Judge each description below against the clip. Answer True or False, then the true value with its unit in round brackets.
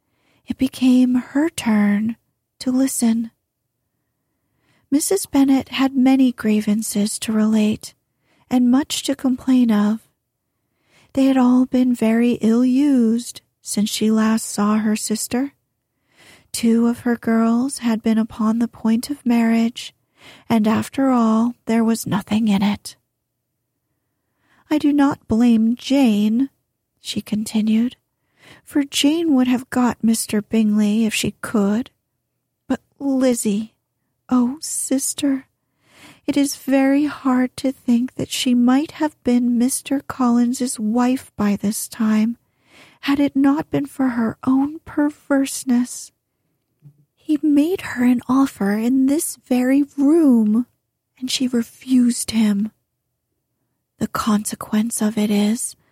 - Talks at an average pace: False (120 wpm)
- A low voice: False (245 Hz)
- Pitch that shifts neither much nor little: True (3.4 semitones)